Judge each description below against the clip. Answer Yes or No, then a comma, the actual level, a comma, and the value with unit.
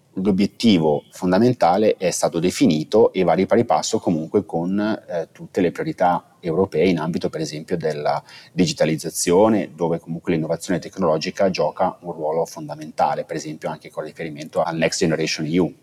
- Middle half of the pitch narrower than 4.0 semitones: No, average, 4.7 semitones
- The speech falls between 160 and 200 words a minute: No, average, 150 wpm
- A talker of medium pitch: No, very low, 85 Hz